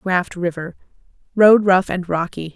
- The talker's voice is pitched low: No, medium, 180 Hz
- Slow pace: Yes, slow, 115 wpm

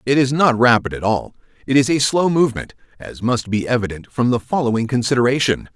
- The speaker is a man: Yes, male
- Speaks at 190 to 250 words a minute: Yes, average, 200 wpm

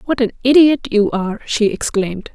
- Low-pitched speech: No, high, 230 Hz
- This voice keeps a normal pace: Yes, average, 180 wpm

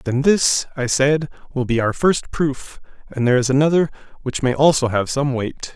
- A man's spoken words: Yes, male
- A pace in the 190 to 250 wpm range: Yes, average, 200 wpm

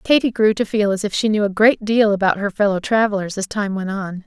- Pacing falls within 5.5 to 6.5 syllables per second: Yes, 5.8 syllables/s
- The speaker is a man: No, female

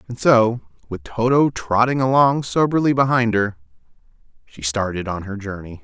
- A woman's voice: No, male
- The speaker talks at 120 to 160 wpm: Yes, average, 145 wpm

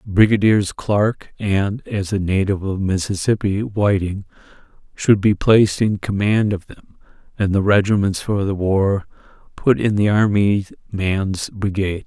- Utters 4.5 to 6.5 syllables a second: No, 3.6 syllables/s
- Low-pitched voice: Yes, low, 100 Hz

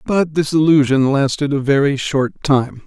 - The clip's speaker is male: Yes, male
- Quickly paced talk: No, average, 165 wpm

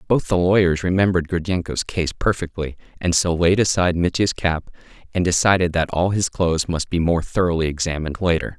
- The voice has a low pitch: Yes, very low, 85 Hz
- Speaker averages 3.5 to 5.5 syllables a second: No, 5.8 syllables/s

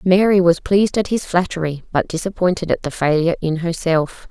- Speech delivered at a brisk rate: No, average, 180 wpm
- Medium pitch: Yes, medium, 175 Hz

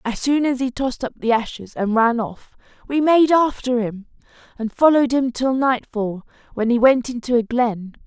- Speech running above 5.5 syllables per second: No, 4.9 syllables/s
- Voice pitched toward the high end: Yes, high, 245 Hz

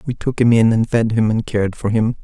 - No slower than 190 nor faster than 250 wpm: No, fast, 295 wpm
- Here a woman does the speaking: No, male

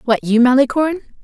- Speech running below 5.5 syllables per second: No, 6.7 syllables/s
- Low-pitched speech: No, very high, 260 Hz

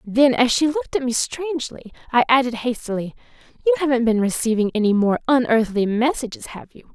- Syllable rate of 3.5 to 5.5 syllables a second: No, 5.8 syllables/s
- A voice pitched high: Yes, very high, 250 Hz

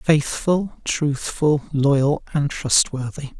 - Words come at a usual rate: No, slow, 90 wpm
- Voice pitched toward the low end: No, medium, 145 Hz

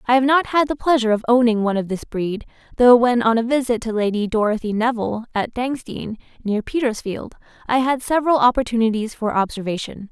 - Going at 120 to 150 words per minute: No, average, 185 wpm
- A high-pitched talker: Yes, high, 235 Hz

